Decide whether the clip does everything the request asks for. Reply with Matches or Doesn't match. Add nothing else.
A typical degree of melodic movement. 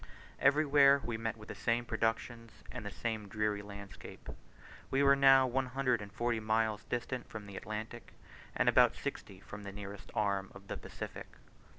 Matches